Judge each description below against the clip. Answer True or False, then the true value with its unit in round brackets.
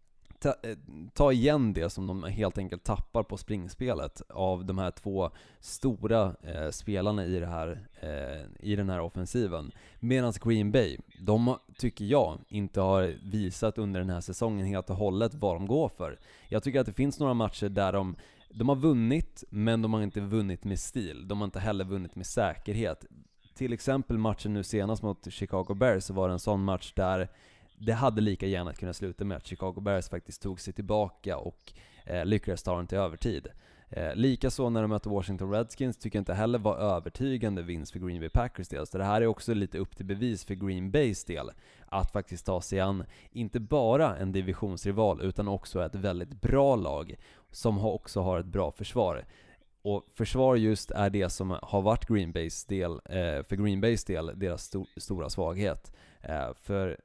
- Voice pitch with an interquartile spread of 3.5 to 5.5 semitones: False (3.0 semitones)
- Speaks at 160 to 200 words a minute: True (195 wpm)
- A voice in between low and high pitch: False (100 Hz)